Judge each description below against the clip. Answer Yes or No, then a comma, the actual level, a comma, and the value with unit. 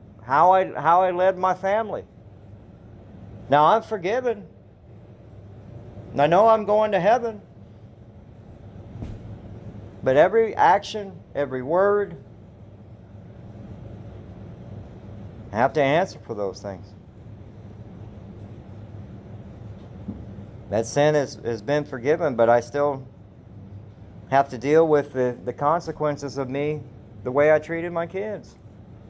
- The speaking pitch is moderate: No, low, 115 Hz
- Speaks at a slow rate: Yes, slow, 105 wpm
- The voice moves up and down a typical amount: No, wide, 6.5 semitones